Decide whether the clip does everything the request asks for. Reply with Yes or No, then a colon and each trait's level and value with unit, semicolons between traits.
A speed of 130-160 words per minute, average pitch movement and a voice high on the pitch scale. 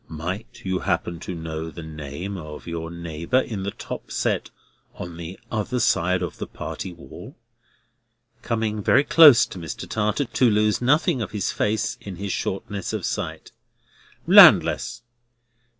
No: average, 150 wpm; average, 4.8 semitones; very low, 95 Hz